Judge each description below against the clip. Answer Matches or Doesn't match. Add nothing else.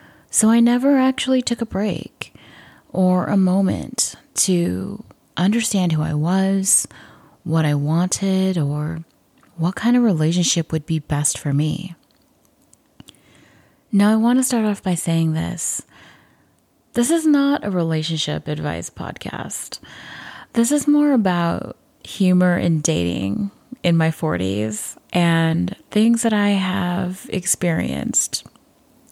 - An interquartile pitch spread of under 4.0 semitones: Doesn't match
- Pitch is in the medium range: Matches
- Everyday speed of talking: Doesn't match